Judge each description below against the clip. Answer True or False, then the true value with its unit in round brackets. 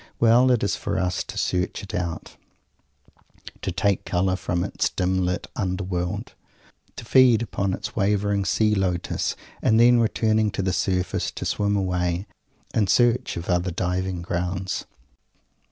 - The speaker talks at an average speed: True (155 wpm)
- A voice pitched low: True (95 Hz)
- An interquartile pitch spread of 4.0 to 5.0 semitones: False (2.9 semitones)